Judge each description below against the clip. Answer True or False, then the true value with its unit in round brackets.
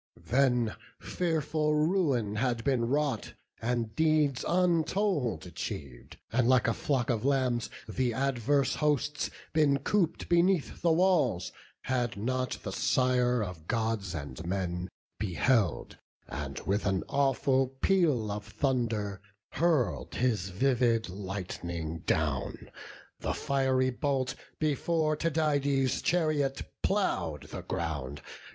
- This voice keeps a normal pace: False (115 wpm)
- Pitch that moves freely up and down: True (6.0 semitones)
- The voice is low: True (130 Hz)